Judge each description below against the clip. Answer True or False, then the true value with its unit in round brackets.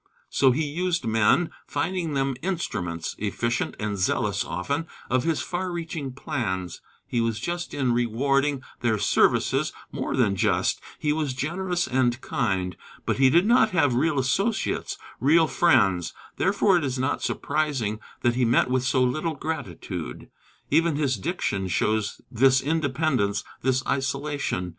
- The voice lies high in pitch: False (135 Hz)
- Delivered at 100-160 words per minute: True (145 wpm)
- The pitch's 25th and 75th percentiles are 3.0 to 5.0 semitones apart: False (5.5 semitones)